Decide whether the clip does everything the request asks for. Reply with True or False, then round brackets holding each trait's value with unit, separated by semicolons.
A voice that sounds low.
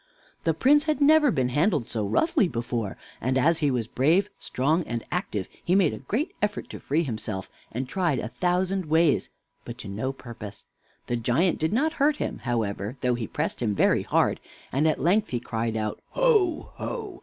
False (145 Hz)